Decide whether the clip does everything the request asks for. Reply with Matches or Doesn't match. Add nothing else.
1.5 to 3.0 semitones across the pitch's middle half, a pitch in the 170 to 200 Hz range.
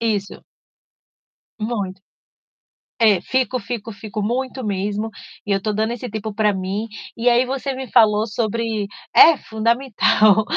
Doesn't match